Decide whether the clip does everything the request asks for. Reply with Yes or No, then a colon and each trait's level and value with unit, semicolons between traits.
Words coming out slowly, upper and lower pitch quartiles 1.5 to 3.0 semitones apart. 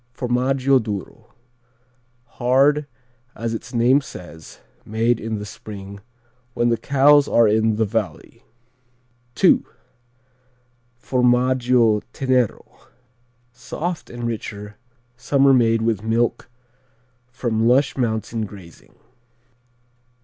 Yes: slow, 95 wpm; average, 2.7 semitones